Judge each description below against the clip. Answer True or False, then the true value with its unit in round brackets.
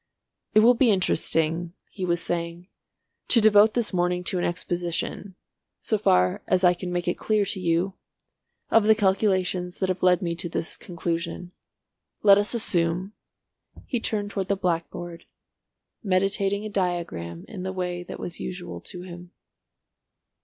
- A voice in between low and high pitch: True (180 Hz)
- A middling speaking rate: True (155 wpm)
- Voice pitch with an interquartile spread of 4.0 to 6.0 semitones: False (2.4 semitones)